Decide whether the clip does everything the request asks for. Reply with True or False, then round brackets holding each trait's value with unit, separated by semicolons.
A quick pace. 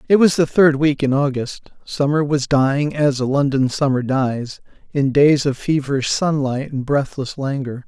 False (175 wpm)